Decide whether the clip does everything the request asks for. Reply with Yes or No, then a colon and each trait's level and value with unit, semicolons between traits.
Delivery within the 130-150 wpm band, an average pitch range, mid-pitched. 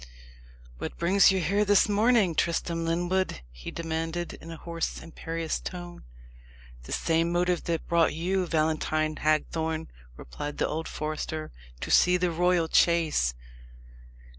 No: slow, 135 wpm; narrow, 1.9 semitones; medium, 165 Hz